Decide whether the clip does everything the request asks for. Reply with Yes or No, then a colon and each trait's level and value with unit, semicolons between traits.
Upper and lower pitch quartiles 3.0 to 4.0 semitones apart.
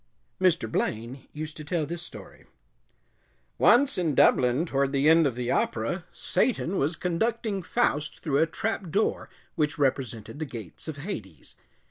No: average, 4.8 semitones